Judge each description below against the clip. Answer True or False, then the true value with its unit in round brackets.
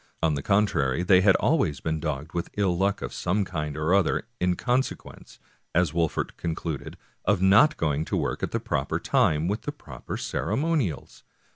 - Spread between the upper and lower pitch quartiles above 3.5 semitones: True (4.7 semitones)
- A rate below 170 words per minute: False (180 wpm)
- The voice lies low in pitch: True (85 Hz)